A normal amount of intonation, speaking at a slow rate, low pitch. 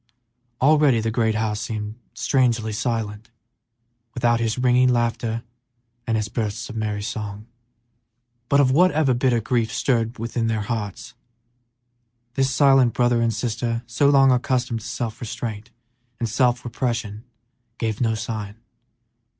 No: narrow, 2.2 semitones; slow, 125 wpm; low, 115 Hz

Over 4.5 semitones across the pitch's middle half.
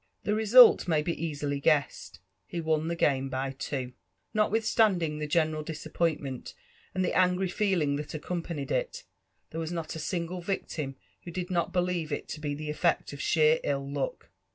No: average, 3.6 semitones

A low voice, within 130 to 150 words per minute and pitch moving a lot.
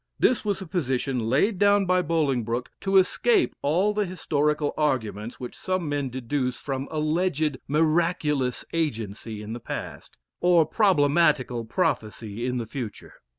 No: medium, 145 Hz; average, 140 wpm; wide, 6.1 semitones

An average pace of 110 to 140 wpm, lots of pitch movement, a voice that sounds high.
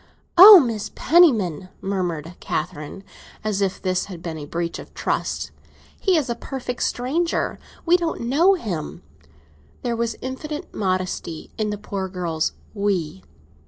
Yes: slow, 135 wpm; wide, 6.5 semitones; high, 205 Hz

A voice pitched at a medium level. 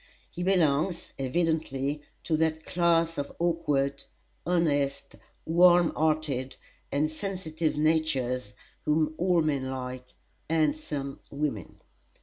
Yes: medium, 155 Hz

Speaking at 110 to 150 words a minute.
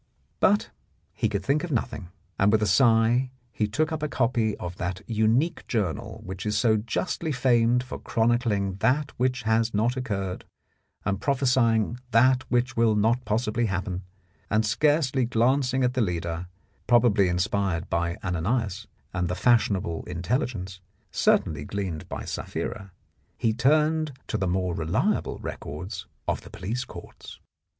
Yes: average, 145 wpm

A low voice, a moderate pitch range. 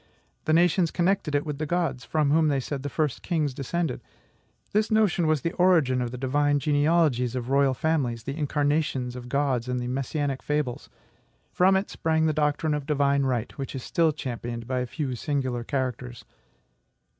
No: medium, 145 Hz; average, 3.7 semitones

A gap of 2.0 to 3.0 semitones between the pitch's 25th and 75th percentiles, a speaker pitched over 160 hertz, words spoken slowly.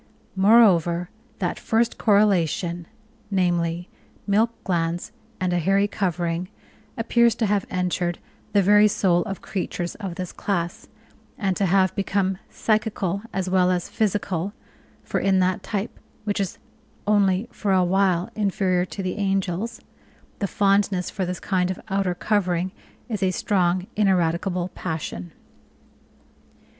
Yes: narrow, 2.4 semitones; high, 190 Hz; slow, 130 wpm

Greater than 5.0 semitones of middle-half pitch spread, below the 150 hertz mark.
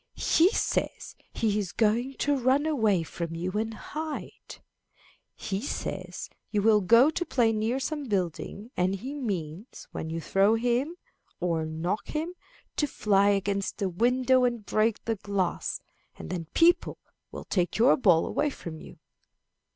No: wide, 5.6 semitones; high, 215 Hz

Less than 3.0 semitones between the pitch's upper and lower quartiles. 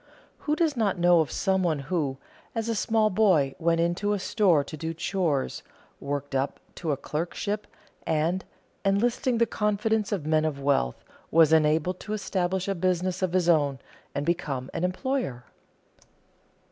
No: average, 4.9 semitones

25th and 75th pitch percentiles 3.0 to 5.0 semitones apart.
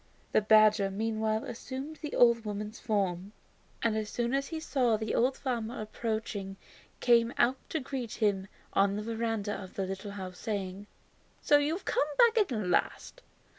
Yes: average, 3.3 semitones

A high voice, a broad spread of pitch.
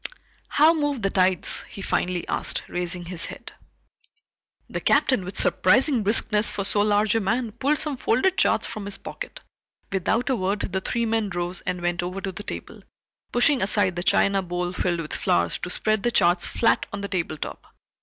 No: high, 200 Hz; average, 4.0 semitones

